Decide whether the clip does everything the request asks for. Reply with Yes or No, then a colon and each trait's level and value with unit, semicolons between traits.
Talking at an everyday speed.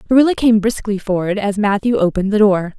Yes: average, 195 wpm